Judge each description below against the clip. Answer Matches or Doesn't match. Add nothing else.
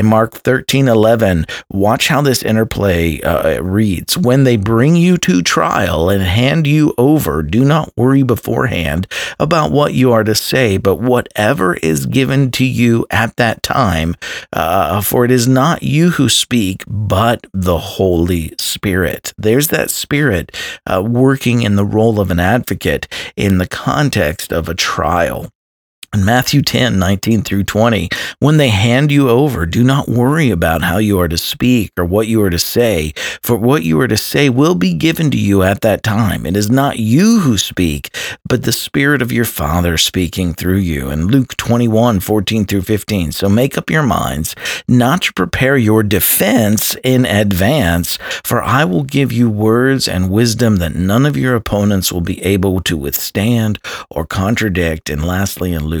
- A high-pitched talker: Doesn't match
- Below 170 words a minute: Doesn't match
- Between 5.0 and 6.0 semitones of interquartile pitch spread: Matches